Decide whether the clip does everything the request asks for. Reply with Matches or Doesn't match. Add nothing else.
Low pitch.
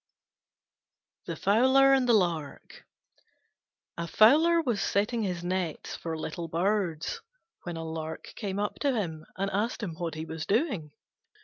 Doesn't match